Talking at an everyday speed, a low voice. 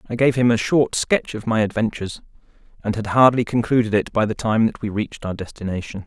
No: fast, 220 wpm; low, 110 Hz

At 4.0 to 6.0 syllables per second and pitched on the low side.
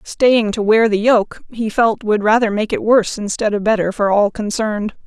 No: 5.0 syllables/s; high, 215 Hz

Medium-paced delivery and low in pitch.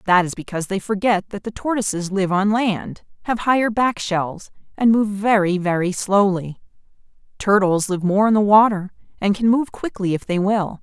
No: average, 185 wpm; high, 200 Hz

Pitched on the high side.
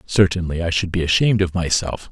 No: very low, 90 Hz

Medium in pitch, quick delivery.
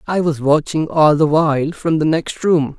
Yes: medium, 155 Hz; fast, 215 wpm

